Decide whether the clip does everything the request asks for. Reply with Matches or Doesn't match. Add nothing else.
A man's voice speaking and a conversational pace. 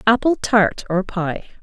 Doesn't match